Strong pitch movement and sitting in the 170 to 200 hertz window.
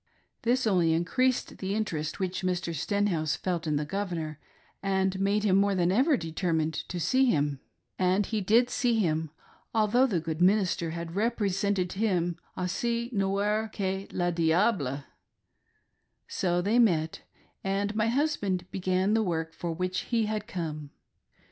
No: average, 4.0 semitones; high, 190 Hz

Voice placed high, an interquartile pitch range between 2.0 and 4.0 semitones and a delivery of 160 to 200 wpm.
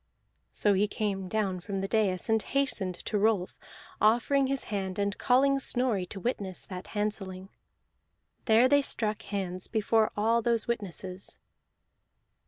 No: high, 210 Hz; average, 3.3 semitones; average, 140 wpm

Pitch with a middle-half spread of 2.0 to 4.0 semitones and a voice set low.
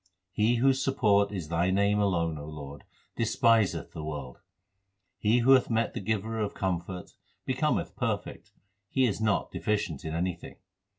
No: average, 5.0 semitones; low, 100 Hz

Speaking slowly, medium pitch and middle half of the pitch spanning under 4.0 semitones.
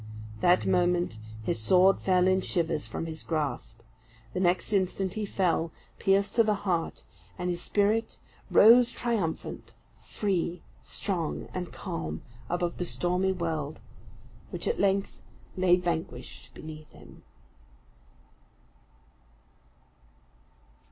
Yes: slow, 110 wpm; medium, 180 Hz; average, 3.0 semitones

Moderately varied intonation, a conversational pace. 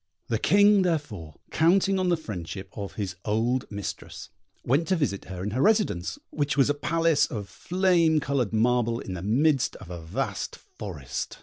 No: wide, 8.5 semitones; average, 175 wpm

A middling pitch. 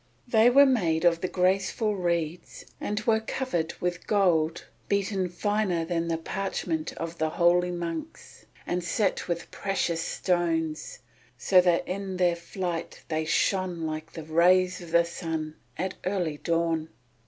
Yes: medium, 175 Hz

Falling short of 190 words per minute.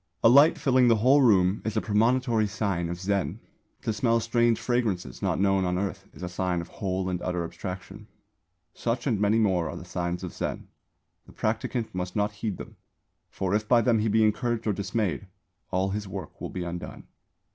No: average, 200 wpm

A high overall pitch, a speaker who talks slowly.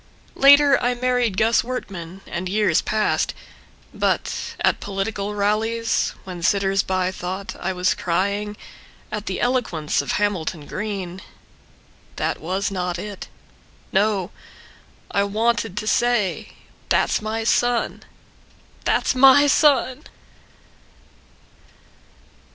Yes: high, 205 Hz; slow, 105 wpm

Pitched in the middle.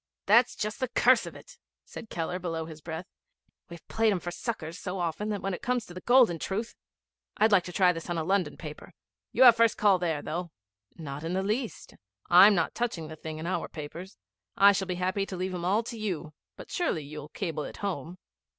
Yes: medium, 180 Hz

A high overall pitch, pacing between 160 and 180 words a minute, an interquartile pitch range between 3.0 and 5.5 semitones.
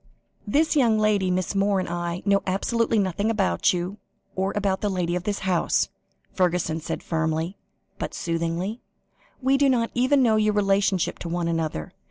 Yes: high, 195 Hz; average, 170 wpm; average, 3.6 semitones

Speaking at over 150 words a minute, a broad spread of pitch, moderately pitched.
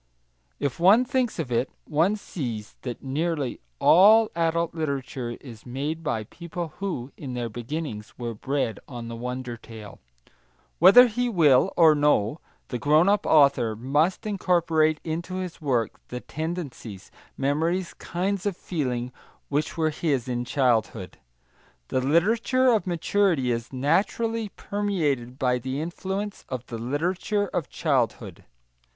No: slow, 135 wpm; wide, 6.3 semitones; medium, 150 Hz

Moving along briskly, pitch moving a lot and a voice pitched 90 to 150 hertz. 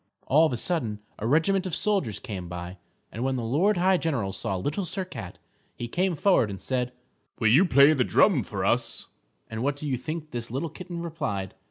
Yes: fast, 215 wpm; wide, 7.2 semitones; low, 135 Hz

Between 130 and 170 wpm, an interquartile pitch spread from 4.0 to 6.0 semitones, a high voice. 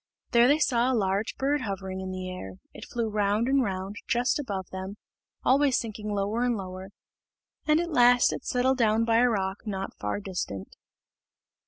No: average, 180 wpm; average, 4.4 semitones; high, 215 Hz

